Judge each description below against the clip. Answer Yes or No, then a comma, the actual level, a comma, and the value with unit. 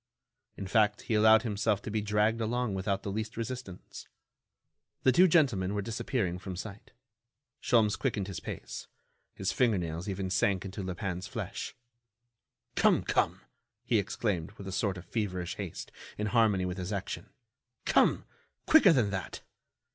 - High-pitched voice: No, low, 100 Hz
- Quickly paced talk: No, average, 155 wpm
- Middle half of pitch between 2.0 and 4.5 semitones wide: Yes, average, 3.0 semitones